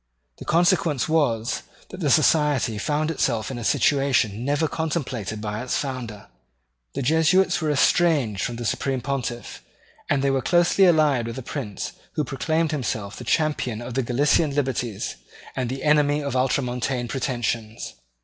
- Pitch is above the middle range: No, low, 135 Hz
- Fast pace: No, average, 155 wpm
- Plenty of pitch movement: No, average, 4.1 semitones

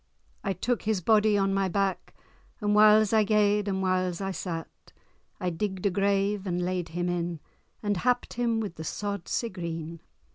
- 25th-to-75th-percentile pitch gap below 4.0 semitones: Yes, average, 2.7 semitones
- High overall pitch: Yes, high, 195 Hz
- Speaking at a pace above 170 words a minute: Yes, average, 180 wpm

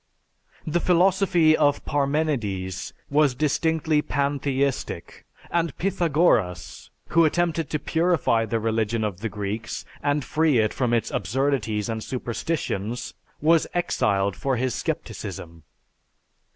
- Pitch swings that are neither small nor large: No, wide, 6.1 semitones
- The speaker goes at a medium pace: No, slow, 110 wpm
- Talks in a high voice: No, medium, 140 Hz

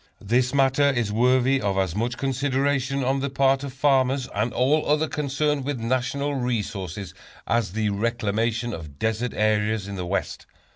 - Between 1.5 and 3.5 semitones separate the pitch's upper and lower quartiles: No, average, 4.2 semitones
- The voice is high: No, low, 125 Hz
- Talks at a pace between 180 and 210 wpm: No, average, 160 wpm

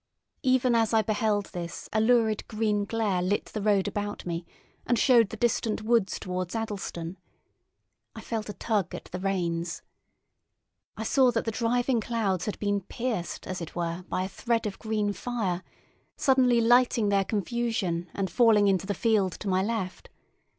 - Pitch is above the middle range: Yes, high, 210 Hz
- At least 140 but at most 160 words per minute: No, average, 170 wpm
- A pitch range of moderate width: Yes, average, 3.4 semitones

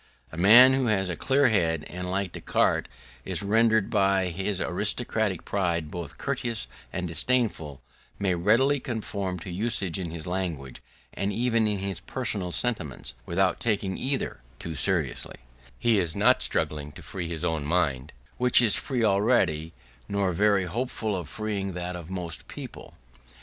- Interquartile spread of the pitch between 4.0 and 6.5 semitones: Yes, average, 4.4 semitones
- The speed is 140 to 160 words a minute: Yes, average, 155 wpm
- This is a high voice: No, very low, 95 Hz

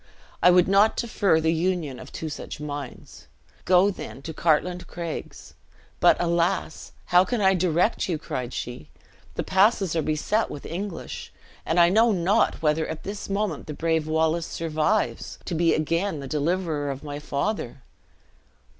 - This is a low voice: No, medium, 170 Hz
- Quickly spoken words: No, average, 165 wpm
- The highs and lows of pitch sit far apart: No, average, 3.6 semitones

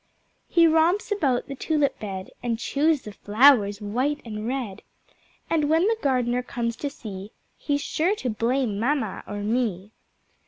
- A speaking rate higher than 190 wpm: No, average, 155 wpm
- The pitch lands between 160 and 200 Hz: No, very high, 250 Hz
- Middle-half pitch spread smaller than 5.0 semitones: No, wide, 5.6 semitones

